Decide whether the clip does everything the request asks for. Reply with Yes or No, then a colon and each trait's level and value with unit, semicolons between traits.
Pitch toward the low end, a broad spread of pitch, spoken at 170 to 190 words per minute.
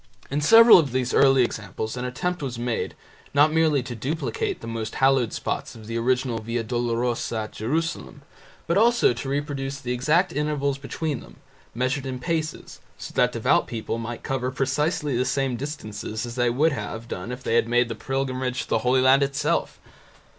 No: low, 130 Hz; average, 3.3 semitones; average, 180 wpm